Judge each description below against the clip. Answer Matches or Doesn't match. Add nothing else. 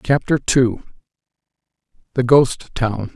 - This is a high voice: Doesn't match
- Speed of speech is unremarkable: Doesn't match